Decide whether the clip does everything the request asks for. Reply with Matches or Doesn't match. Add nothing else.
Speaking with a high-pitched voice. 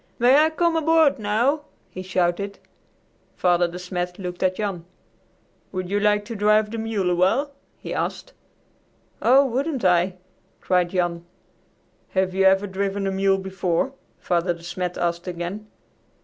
Matches